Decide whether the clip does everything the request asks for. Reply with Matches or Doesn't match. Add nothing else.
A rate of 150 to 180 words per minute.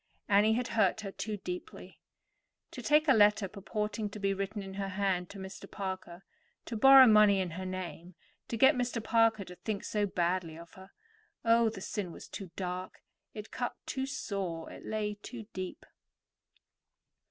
Matches